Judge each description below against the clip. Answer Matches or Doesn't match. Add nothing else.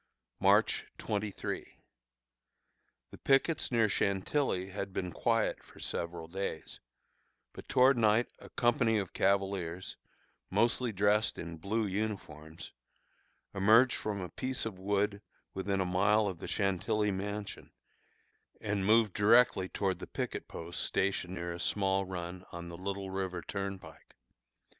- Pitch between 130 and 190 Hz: Doesn't match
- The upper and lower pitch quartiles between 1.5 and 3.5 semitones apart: Matches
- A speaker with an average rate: Doesn't match